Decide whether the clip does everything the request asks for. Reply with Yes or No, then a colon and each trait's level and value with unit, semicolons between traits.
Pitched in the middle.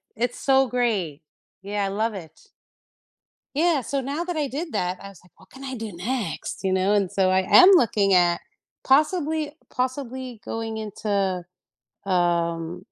No: high, 215 Hz